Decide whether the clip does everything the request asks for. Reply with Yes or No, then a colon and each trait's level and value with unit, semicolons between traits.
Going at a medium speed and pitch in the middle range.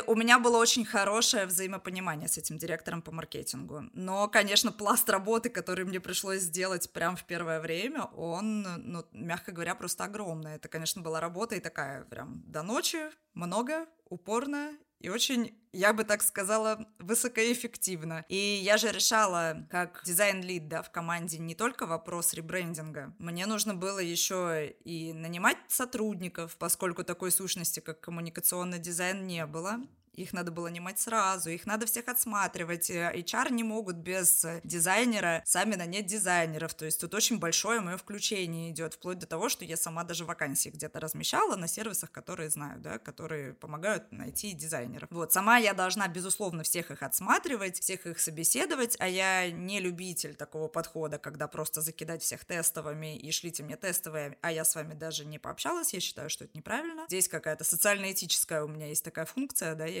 No: fast, 165 wpm; medium, 180 Hz